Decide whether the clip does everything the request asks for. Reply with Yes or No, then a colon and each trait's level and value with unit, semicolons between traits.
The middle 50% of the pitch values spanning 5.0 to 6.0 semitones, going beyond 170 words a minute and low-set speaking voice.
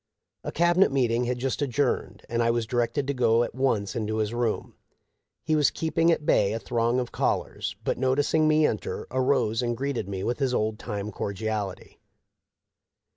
No: average, 3.7 semitones; average, 180 wpm; low, 120 Hz